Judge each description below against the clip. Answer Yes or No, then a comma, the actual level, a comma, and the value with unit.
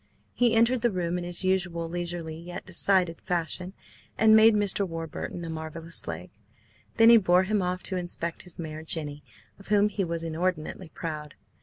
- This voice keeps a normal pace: Yes, average, 175 wpm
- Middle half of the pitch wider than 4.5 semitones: No, average, 2.9 semitones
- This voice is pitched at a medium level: Yes, medium, 175 Hz